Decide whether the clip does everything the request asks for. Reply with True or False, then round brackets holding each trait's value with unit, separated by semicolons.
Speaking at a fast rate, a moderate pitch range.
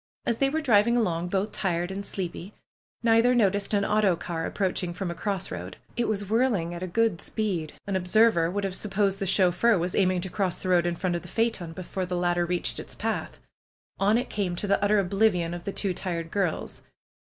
True (220 wpm; 3.2 semitones)